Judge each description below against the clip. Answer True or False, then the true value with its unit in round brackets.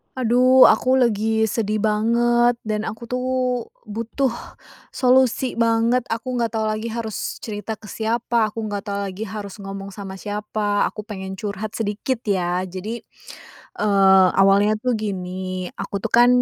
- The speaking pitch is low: False (215 Hz)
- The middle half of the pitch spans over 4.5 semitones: False (2.7 semitones)